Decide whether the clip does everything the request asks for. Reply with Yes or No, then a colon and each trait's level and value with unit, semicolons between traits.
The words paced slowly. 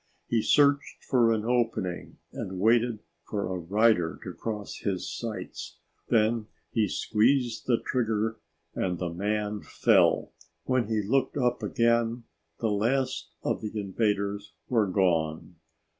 Yes: slow, 130 wpm